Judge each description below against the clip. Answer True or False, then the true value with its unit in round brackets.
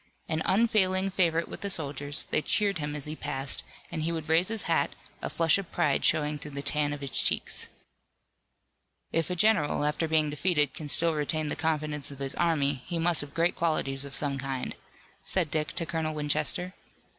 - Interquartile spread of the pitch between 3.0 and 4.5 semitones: False (2.5 semitones)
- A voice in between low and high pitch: True (155 Hz)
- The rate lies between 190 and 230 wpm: True (195 wpm)